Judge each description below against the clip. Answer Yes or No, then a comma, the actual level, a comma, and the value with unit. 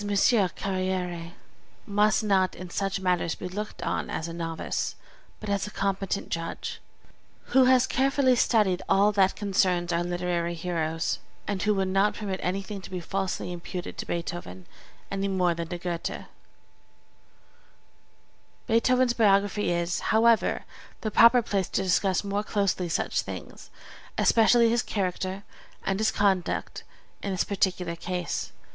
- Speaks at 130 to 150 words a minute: Yes, average, 140 wpm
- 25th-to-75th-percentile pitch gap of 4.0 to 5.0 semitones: No, average, 2.8 semitones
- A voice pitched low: No, high, 190 Hz